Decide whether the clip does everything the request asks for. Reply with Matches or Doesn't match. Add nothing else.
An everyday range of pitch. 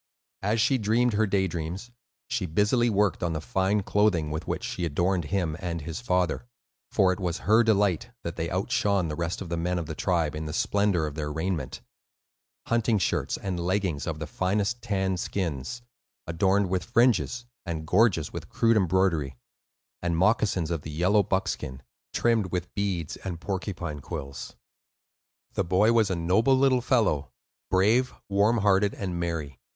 Matches